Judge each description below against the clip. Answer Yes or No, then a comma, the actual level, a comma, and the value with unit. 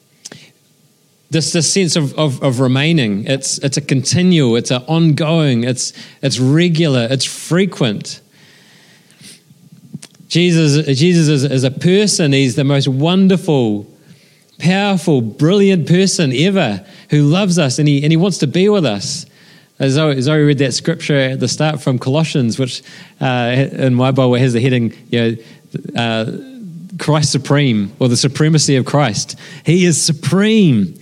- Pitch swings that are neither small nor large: Yes, average, 4.3 semitones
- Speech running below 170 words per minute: Yes, average, 145 wpm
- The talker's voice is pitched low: No, medium, 150 Hz